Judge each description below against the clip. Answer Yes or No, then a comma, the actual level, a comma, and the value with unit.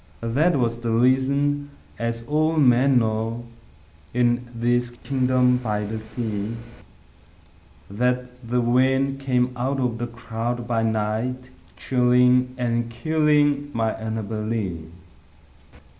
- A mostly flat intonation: Yes, narrow, 2.2 semitones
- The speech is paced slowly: Yes, slow, 115 wpm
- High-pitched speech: No, low, 120 Hz